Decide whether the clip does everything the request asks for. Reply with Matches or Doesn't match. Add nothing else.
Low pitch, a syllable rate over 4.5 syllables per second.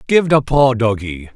Doesn't match